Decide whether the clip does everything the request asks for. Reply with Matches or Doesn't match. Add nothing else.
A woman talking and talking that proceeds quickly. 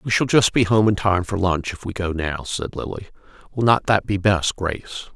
Doesn't match